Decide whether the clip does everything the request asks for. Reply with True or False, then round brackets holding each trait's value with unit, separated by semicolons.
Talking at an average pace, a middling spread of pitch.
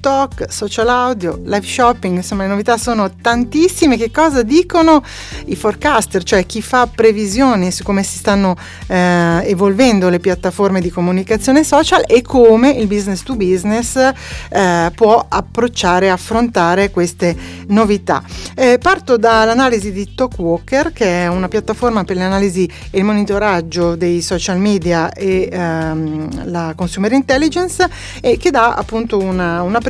True (140 wpm; 5.0 semitones)